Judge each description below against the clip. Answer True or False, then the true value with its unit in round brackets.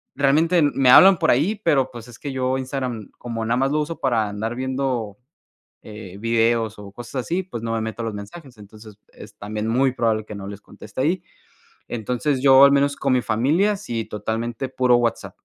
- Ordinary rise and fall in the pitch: True (3.6 semitones)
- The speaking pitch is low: True (120 Hz)